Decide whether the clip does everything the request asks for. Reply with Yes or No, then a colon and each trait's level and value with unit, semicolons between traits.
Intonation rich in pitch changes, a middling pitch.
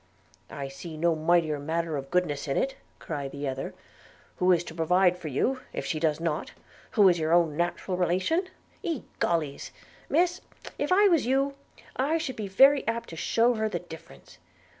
Yes: wide, 7.4 semitones; medium, 175 Hz